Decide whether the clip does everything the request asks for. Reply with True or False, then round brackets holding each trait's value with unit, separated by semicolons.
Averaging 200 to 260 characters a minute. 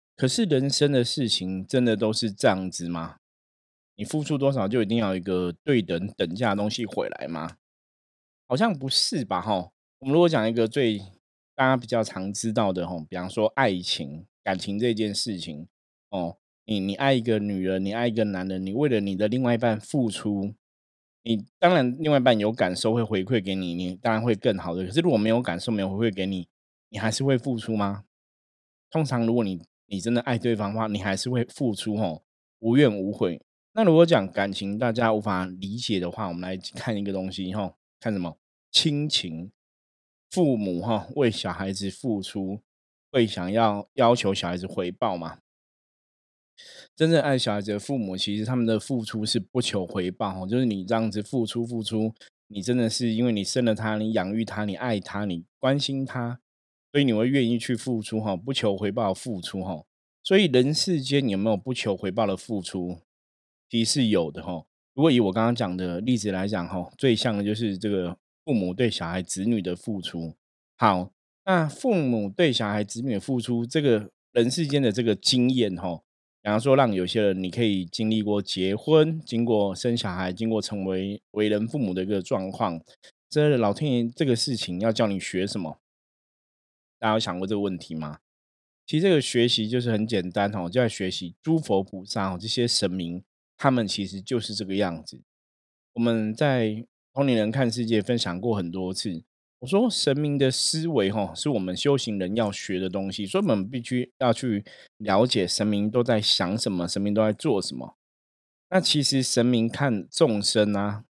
False (275 characters per minute)